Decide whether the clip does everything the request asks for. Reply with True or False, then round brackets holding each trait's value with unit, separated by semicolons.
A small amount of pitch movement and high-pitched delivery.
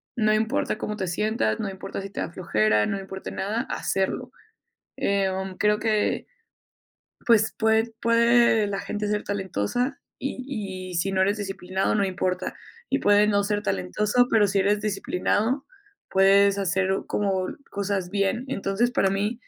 True (2.3 semitones; 200 Hz)